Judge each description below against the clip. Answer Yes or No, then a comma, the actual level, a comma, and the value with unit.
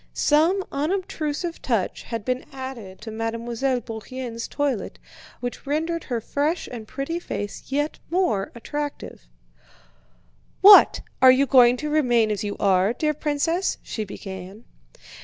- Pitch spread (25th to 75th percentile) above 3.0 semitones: Yes, average, 5.0 semitones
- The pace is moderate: No, slow, 130 wpm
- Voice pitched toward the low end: No, very high, 255 Hz